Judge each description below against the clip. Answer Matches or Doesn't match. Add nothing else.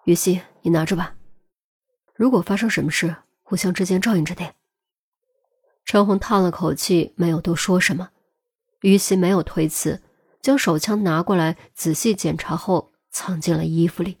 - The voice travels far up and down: Doesn't match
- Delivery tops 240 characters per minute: Doesn't match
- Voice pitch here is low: Doesn't match